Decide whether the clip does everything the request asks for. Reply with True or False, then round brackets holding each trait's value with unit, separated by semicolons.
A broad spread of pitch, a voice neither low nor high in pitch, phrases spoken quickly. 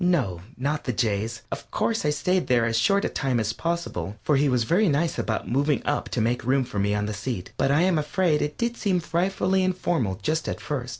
True (6.9 semitones; 145 Hz; 235 wpm)